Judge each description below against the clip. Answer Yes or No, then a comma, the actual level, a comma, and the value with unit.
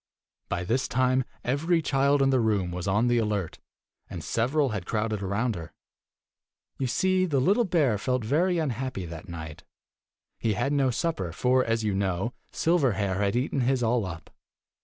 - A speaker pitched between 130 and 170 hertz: No, low, 120 Hz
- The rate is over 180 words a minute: No, average, 175 wpm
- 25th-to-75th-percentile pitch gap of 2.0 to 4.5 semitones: No, wide, 5.4 semitones